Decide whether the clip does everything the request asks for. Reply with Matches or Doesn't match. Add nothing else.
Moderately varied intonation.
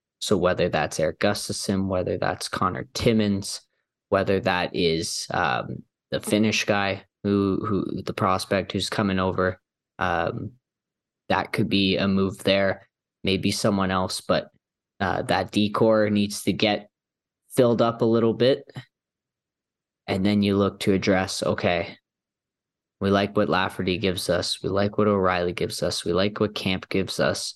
Doesn't match